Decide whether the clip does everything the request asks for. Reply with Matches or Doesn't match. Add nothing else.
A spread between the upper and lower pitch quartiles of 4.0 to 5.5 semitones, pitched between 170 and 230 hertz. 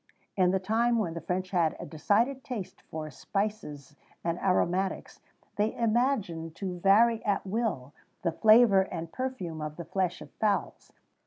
Matches